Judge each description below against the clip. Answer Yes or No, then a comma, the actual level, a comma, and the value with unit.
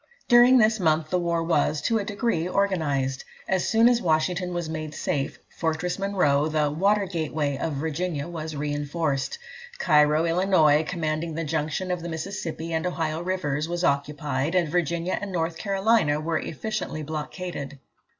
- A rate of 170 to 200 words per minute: No, average, 155 wpm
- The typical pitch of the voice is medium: Yes, medium, 165 Hz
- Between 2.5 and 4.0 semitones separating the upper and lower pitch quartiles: Yes, average, 3.3 semitones